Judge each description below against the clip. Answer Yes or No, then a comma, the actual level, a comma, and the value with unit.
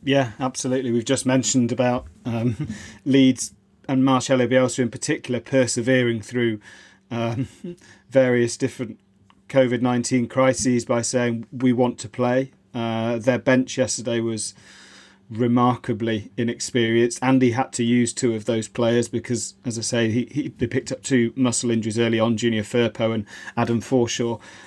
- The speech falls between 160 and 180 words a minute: No, average, 150 wpm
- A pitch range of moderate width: No, narrow, 2.0 semitones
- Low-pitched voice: Yes, low, 120 Hz